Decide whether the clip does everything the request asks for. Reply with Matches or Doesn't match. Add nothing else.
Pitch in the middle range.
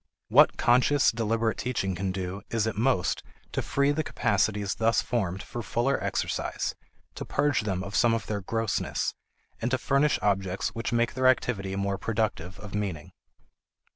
Doesn't match